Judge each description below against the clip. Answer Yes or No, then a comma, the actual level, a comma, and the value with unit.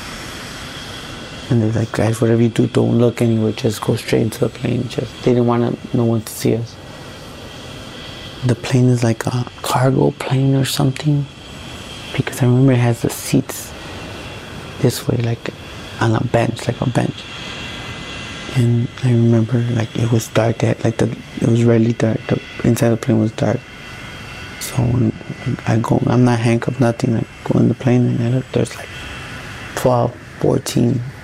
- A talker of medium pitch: No, low, 120 Hz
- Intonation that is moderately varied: No, narrow, 1.7 semitones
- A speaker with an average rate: Yes, average, 175 wpm